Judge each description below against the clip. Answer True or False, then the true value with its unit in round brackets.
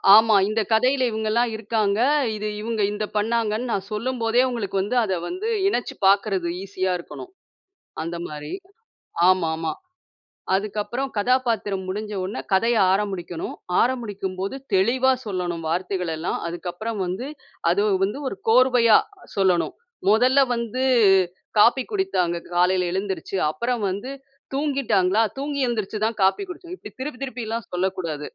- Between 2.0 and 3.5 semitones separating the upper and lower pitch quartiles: False (4.3 semitones)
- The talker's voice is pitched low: False (215 Hz)